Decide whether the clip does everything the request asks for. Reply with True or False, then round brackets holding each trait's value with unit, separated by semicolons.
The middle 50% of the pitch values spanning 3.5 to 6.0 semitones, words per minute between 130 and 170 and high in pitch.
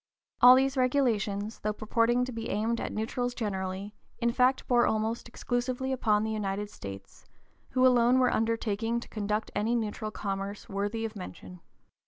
False (2.9 semitones; 160 wpm; 225 Hz)